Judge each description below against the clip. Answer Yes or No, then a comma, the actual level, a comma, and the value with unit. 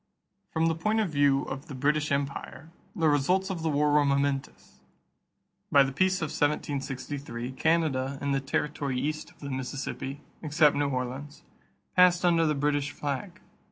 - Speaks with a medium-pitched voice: Yes, medium, 145 Hz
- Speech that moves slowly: No, average, 160 wpm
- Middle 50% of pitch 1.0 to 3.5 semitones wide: Yes, narrow, 2.6 semitones